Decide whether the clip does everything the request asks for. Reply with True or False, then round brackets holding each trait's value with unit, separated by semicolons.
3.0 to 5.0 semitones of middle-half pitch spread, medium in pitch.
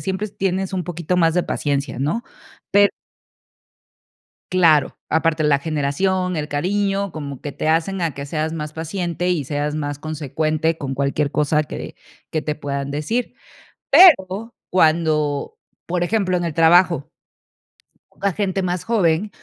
True (3.8 semitones; 165 Hz)